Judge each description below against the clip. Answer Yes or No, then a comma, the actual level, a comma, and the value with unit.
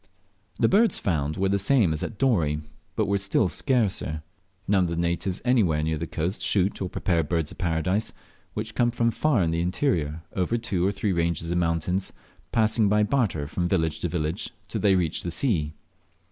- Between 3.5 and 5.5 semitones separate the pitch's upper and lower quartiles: Yes, average, 4.5 semitones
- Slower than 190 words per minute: No, average, 195 wpm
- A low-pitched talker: Yes, very low, 90 Hz